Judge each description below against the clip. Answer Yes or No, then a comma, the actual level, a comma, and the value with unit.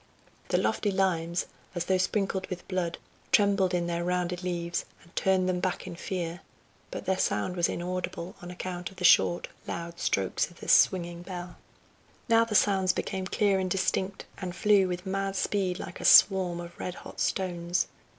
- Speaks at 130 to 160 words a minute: No, average, 180 wpm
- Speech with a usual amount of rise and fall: No, narrow, 1.6 semitones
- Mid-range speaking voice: Yes, medium, 180 Hz